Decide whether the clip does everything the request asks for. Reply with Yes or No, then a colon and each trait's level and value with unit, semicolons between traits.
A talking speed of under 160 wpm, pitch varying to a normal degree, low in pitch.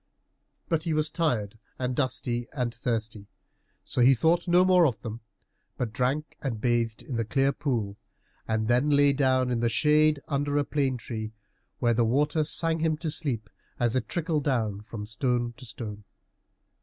No: average, 175 wpm; average, 4.6 semitones; low, 125 Hz